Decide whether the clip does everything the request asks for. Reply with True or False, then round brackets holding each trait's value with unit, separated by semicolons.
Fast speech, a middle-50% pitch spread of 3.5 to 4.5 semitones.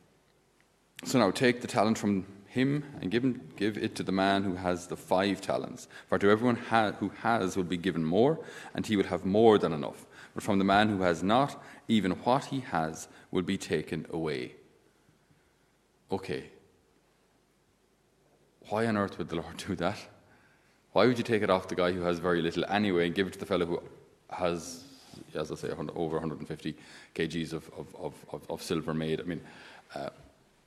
False (185 wpm; 3.9 semitones)